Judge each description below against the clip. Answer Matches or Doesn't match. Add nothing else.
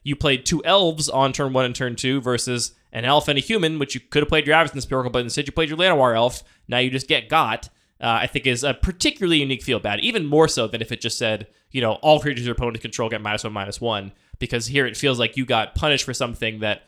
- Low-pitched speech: Matches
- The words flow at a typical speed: Doesn't match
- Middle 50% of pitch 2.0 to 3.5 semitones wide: Doesn't match